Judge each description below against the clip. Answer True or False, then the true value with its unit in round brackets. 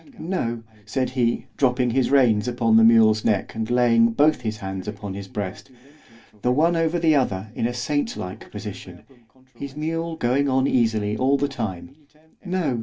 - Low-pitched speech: True (120 Hz)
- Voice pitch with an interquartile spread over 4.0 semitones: True (4.5 semitones)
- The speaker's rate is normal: True (175 wpm)